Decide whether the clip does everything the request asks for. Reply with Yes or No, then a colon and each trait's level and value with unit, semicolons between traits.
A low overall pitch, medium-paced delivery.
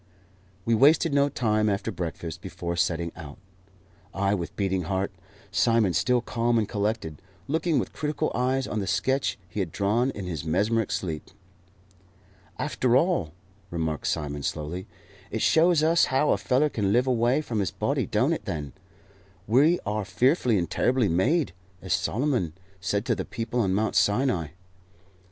Yes: low, 105 Hz; average, 160 wpm